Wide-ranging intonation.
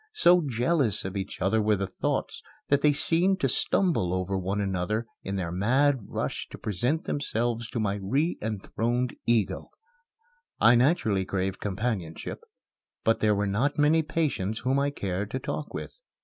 Yes: wide, 6.4 semitones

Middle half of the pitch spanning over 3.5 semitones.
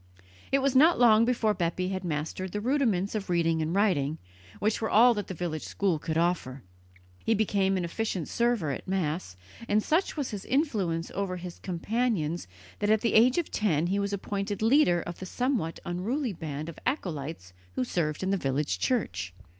Yes: average, 5.2 semitones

